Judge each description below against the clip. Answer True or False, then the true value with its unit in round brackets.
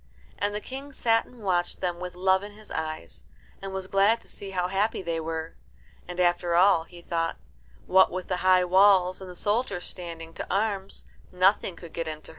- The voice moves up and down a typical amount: False (2.3 semitones)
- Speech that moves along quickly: True (215 wpm)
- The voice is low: False (185 Hz)